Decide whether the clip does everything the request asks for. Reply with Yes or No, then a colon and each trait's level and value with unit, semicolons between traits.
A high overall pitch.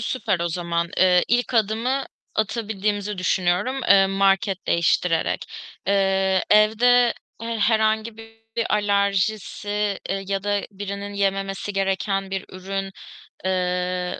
Yes: high, 195 Hz